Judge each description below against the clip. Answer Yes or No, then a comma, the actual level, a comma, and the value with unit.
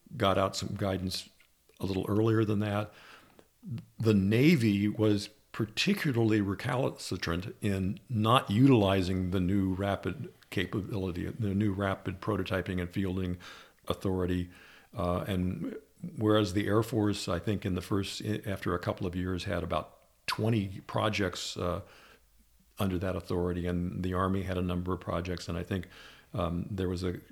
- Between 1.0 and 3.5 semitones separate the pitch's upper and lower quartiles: Yes, average, 2.7 semitones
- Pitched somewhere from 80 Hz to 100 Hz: Yes, very low, 95 Hz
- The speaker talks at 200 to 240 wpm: No, average, 145 wpm